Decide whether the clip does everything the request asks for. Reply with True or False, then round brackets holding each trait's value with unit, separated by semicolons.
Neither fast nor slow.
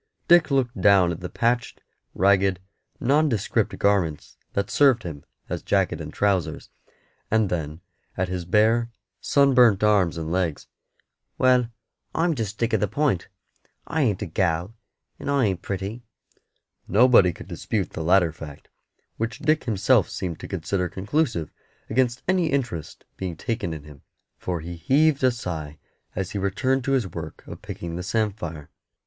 True (155 wpm)